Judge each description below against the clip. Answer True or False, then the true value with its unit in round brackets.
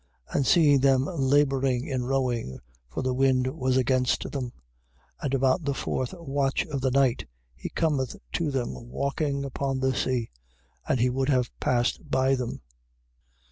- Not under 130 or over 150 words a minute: False (160 wpm)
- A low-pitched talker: True (130 Hz)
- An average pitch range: False (1.6 semitones)